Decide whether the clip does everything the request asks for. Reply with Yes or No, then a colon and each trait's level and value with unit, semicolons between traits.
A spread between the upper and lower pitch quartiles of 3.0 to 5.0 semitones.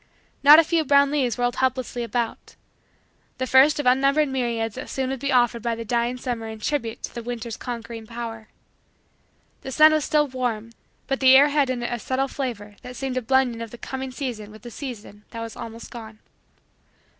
No: narrow, 2.6 semitones